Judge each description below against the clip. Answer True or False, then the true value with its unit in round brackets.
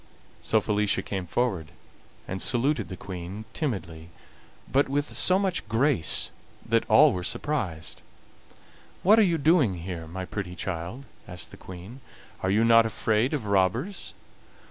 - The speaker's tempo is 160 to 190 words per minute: False (145 wpm)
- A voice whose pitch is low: True (105 Hz)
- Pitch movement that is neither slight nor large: False (7.0 semitones)